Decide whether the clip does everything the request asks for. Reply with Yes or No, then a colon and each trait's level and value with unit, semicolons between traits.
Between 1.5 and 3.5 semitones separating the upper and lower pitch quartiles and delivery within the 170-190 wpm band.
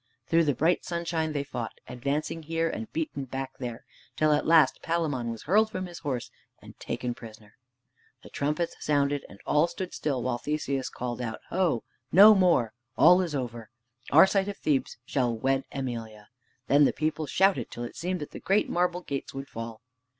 No: average, 5.3 semitones; average, 180 wpm